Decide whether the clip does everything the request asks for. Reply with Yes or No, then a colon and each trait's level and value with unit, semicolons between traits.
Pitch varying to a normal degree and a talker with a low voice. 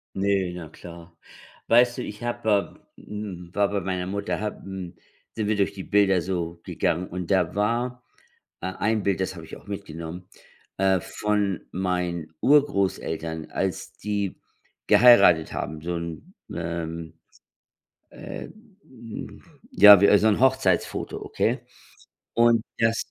Yes: average, 3.4 semitones; very low, 95 Hz